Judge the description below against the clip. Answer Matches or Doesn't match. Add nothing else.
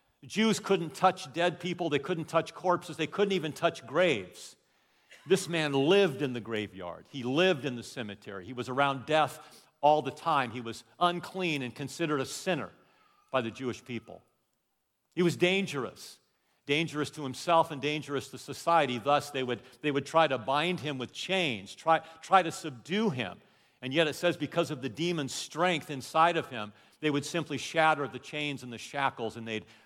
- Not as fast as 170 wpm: Doesn't match